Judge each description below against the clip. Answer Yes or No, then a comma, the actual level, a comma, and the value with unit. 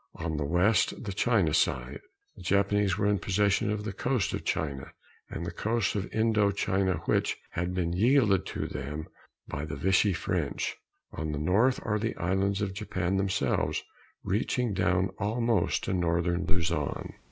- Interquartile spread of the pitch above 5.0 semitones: No, average, 3.2 semitones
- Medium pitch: No, very low, 95 Hz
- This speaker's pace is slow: No, average, 165 wpm